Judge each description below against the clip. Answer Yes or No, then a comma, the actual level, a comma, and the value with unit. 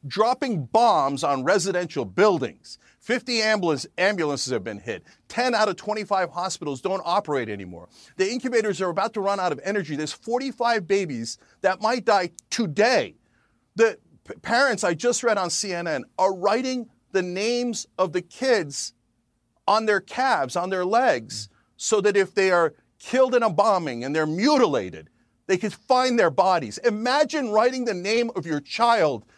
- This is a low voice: No, high, 195 Hz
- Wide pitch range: Yes, wide, 6.2 semitones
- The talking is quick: No, average, 160 wpm